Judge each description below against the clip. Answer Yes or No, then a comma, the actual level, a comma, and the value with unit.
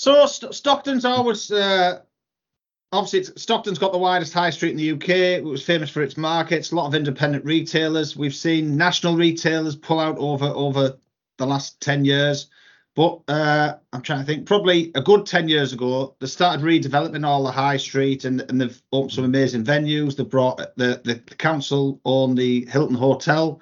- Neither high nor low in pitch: Yes, medium, 150 Hz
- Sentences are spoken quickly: No, average, 190 wpm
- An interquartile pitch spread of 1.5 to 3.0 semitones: No, average, 3.7 semitones